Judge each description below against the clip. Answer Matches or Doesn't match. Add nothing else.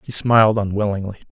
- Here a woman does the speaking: Doesn't match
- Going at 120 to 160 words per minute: Matches